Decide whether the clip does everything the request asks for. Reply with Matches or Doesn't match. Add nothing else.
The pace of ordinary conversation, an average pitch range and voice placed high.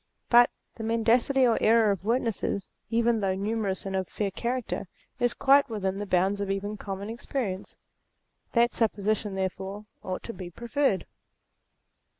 Matches